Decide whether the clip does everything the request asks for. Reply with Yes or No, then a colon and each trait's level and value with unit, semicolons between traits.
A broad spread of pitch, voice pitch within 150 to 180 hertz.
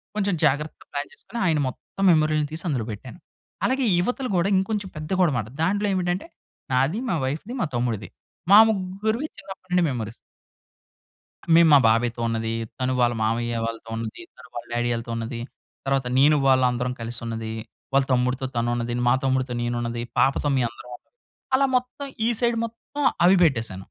No: wide, 7.7 semitones; low, 135 Hz